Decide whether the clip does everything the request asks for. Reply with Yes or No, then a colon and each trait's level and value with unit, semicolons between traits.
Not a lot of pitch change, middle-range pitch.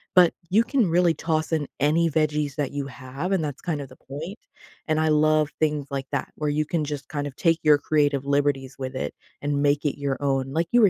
Yes: narrow, 2.2 semitones; medium, 150 Hz